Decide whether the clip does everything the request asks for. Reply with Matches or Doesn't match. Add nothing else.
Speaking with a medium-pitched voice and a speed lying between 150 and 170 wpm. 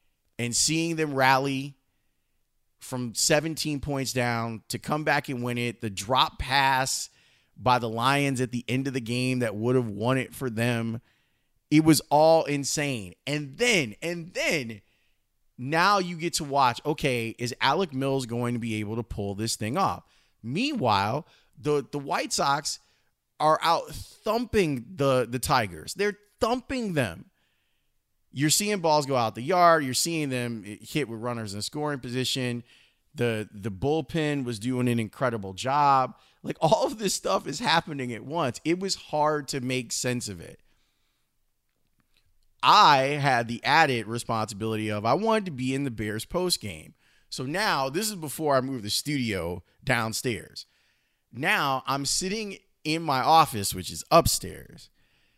Doesn't match